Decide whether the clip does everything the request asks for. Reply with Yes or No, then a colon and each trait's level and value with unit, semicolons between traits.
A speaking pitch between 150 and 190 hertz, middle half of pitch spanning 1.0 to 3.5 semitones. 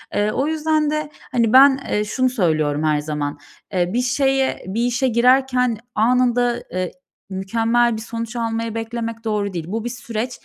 No: high, 230 Hz; average, 3.2 semitones